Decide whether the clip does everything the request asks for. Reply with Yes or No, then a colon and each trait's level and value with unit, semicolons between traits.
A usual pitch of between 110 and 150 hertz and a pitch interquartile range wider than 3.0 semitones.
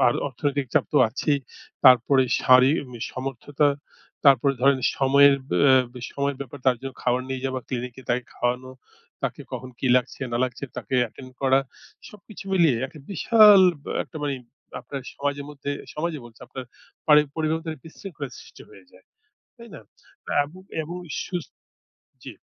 No: medium, 140 Hz; average, 2.7 semitones